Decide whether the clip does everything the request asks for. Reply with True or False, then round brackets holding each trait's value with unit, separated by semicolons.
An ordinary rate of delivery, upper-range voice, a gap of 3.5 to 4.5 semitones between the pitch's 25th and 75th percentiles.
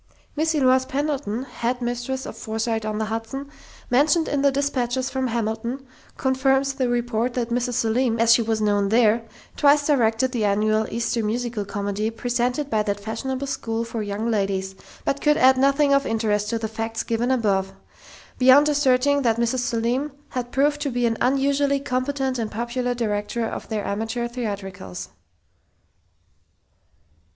False (160 wpm; 240 Hz; 3.1 semitones)